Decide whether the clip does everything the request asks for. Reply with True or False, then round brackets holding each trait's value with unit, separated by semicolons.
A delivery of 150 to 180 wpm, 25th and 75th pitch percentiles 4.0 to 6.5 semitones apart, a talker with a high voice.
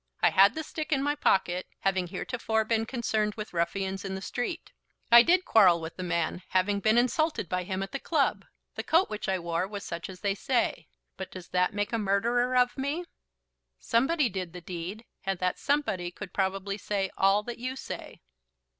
False (200 wpm; 4.8 semitones; 200 Hz)